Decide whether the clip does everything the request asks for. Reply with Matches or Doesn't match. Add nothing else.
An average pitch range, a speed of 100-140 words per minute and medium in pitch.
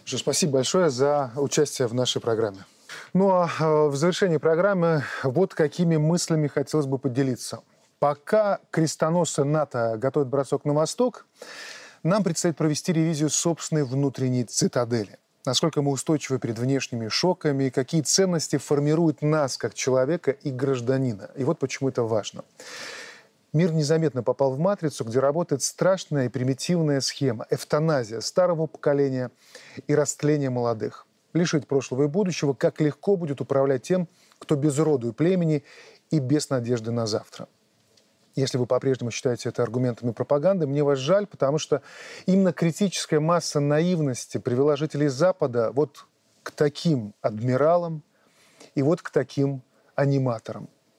Matches